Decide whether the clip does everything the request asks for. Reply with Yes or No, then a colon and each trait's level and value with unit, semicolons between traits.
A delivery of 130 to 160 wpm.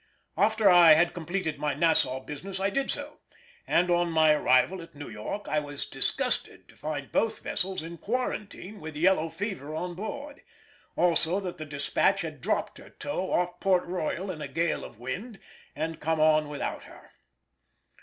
No: average, 175 wpm